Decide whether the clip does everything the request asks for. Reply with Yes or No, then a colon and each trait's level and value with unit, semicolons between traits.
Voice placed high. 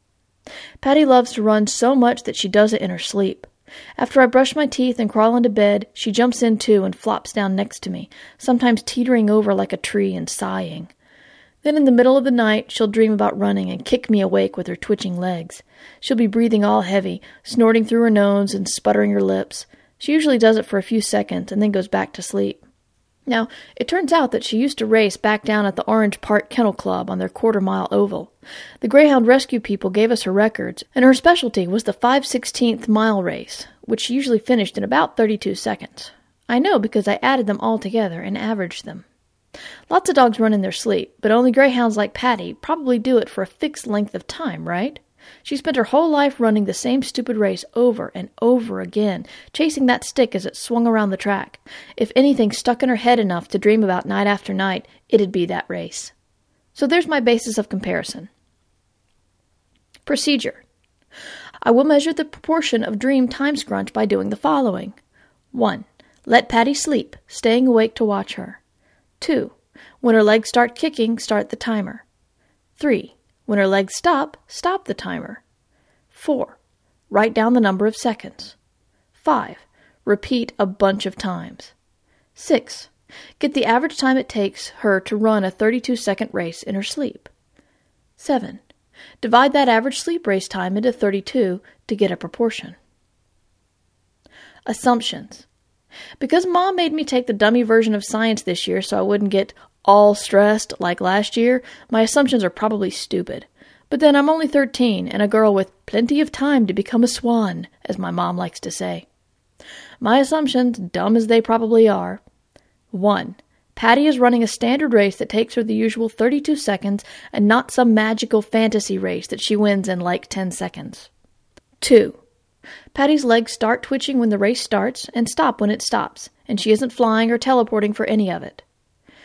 Yes: high, 225 Hz